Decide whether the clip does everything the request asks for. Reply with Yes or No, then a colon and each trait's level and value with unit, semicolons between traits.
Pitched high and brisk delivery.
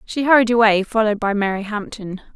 No: high, 215 Hz; average, 180 wpm